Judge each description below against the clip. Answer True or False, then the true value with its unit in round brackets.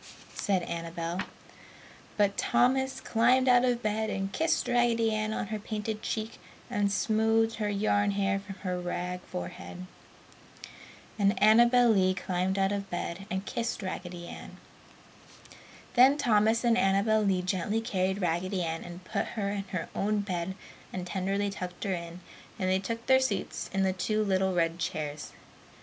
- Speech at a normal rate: True (160 wpm)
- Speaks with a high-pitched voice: True (200 Hz)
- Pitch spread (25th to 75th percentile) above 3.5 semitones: False (3.2 semitones)